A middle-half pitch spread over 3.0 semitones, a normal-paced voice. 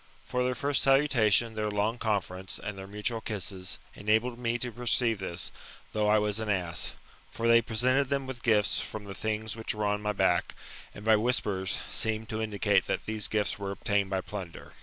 No: narrow, 2.4 semitones; average, 195 wpm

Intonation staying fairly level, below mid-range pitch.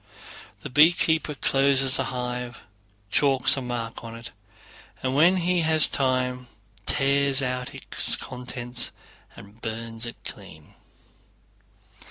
Yes: narrow, 2.3 semitones; low, 130 Hz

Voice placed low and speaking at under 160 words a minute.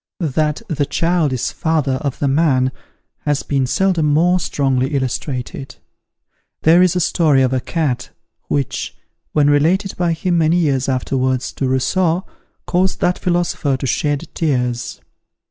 No: medium, 145 Hz; average, 145 wpm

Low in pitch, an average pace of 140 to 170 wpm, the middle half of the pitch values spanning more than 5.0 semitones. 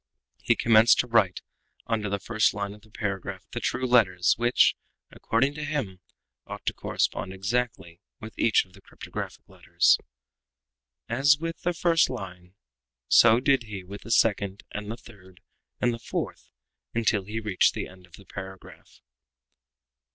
No: low, 110 Hz; average, 160 wpm; average, 3.9 semitones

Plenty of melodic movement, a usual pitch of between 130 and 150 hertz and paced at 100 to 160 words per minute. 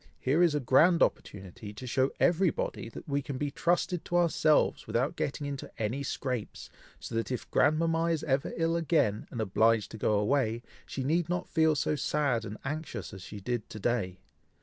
No: wide, 6.1 semitones; medium, 140 Hz; average, 190 wpm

